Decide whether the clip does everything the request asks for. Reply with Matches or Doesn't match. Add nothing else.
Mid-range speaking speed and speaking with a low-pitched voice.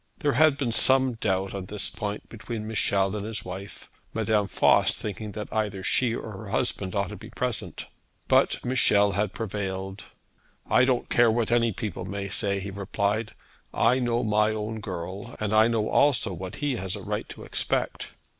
Matches